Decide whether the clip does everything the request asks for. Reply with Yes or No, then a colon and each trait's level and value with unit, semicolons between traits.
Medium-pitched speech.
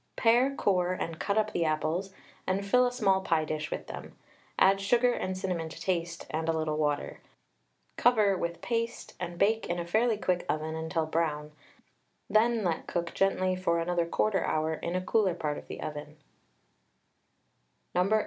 Yes: medium, 180 Hz